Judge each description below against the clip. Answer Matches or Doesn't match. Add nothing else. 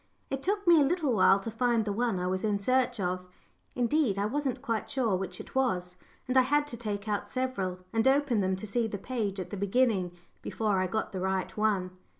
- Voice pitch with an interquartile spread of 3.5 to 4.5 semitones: Doesn't match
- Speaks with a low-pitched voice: Doesn't match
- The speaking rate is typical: Doesn't match